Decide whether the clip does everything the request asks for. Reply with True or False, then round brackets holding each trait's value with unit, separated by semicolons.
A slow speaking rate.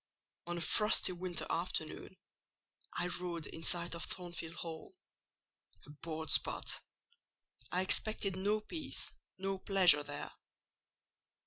True (105 wpm)